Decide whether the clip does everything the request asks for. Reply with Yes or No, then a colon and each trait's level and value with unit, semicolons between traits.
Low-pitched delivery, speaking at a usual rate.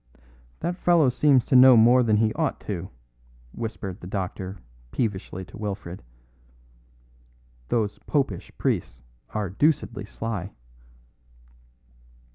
No: low, 110 Hz; slow, 105 wpm